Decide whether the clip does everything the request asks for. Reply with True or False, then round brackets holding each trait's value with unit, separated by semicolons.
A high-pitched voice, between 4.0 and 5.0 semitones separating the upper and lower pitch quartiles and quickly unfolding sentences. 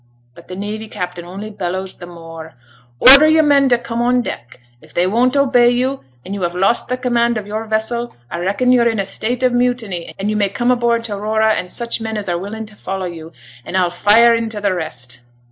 True (215 Hz; 4.6 semitones; 230 wpm)